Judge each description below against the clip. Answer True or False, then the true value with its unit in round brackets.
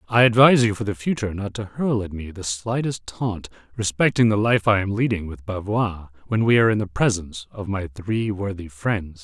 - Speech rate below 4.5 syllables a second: False (5.4 syllables/s)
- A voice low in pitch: True (100 Hz)